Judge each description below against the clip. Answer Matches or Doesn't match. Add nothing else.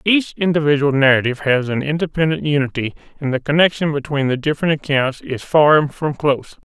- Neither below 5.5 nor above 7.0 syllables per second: Matches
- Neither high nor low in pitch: Matches